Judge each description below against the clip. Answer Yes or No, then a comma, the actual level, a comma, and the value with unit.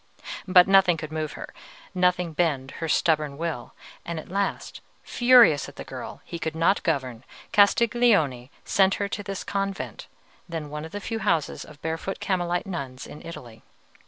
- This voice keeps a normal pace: Yes, average, 165 wpm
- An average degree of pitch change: Yes, average, 4.3 semitones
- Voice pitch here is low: No, medium, 170 Hz